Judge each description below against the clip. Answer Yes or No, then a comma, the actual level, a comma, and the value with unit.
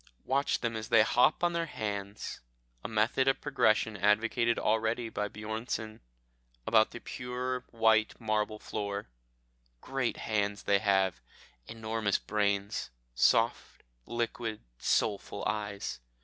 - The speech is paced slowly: Yes, slow, 120 wpm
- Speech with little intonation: Yes, narrow, 2.2 semitones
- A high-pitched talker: No, low, 110 Hz